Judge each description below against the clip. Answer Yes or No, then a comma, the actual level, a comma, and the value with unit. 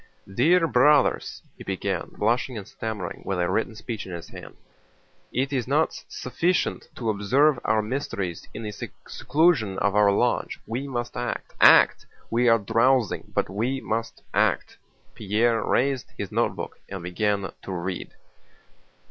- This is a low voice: Yes, low, 115 Hz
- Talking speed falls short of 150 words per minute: Yes, average, 140 wpm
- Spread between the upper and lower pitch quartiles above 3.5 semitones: Yes, average, 4.4 semitones